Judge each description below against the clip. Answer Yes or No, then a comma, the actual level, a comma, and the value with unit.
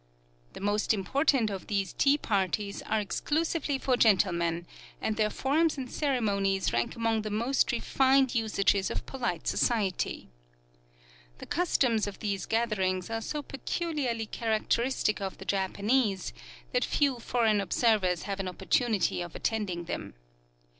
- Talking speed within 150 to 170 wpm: No, slow, 135 wpm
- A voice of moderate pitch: No, high, 220 Hz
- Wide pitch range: No, average, 4.6 semitones